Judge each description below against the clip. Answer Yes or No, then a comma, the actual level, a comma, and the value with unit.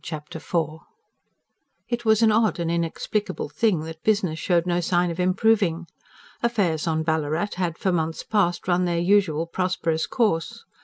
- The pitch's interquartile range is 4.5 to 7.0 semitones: No, average, 3.8 semitones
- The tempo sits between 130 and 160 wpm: Yes, average, 155 wpm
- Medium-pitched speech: Yes, medium, 175 Hz